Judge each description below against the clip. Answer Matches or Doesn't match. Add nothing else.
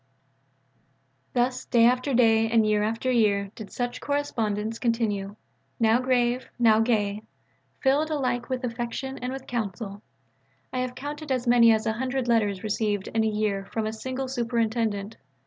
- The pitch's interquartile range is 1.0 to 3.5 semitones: Matches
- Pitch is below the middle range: Doesn't match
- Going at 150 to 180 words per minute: Matches